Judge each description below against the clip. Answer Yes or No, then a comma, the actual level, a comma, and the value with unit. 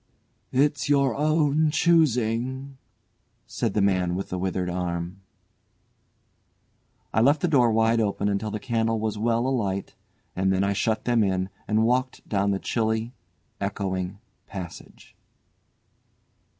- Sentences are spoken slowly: Yes, slow, 130 wpm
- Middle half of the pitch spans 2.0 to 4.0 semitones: No, average, 4.8 semitones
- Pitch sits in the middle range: No, low, 110 Hz